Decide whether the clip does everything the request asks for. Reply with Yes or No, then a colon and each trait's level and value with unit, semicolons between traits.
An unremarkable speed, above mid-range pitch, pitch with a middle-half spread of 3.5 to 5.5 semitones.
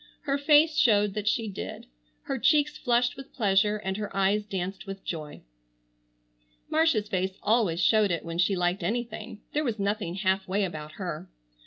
Yes: average, 170 wpm; high, 205 Hz; average, 3.9 semitones